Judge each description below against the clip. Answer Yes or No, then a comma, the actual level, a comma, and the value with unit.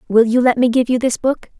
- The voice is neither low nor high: No, high, 245 Hz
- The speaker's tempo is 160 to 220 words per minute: No, fast, 300 wpm